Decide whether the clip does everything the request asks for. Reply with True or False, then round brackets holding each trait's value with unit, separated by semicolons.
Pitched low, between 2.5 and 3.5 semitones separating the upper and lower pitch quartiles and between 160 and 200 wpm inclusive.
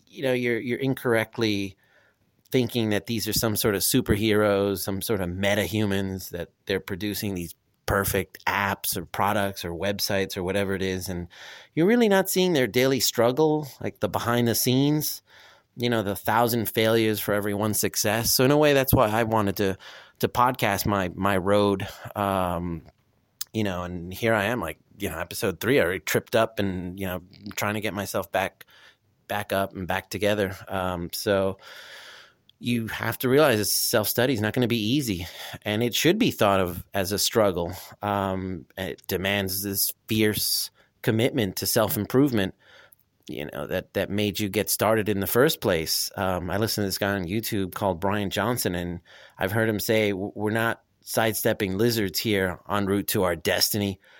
True (105 Hz; 2.8 semitones; 185 wpm)